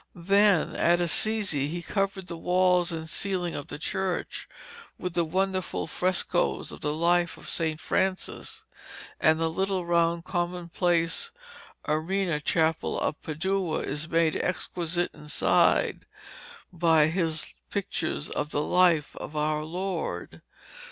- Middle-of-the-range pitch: Yes, medium, 170 Hz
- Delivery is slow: Yes, slow, 125 wpm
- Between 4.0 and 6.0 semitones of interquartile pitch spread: No, narrow, 2.6 semitones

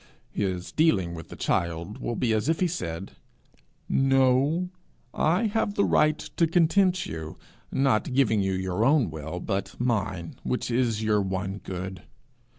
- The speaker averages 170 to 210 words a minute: No, average, 155 wpm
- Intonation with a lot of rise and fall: Yes, wide, 8.4 semitones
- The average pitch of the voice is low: Yes, low, 110 Hz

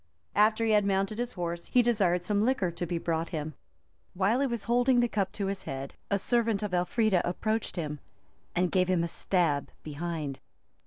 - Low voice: No, high, 190 Hz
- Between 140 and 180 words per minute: No, average, 195 wpm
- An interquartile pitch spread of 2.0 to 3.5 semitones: No, average, 4.3 semitones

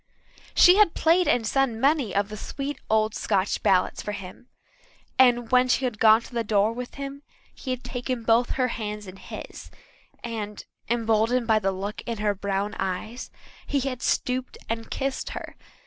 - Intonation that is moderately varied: Yes, average, 3.3 semitones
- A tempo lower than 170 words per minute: No, average, 180 wpm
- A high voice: Yes, high, 230 Hz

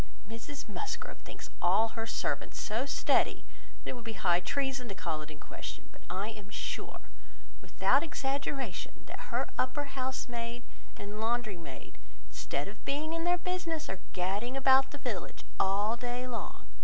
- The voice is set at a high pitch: Yes, high, 240 Hz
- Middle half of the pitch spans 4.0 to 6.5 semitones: Yes, average, 5.1 semitones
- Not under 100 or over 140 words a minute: No, average, 165 wpm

